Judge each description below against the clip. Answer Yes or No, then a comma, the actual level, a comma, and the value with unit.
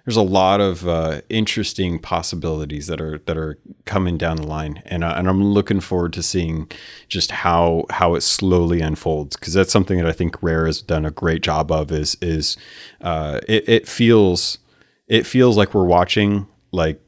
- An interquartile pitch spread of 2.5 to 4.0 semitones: Yes, average, 3.7 semitones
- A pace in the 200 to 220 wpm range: No, average, 190 wpm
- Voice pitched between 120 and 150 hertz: No, very low, 85 Hz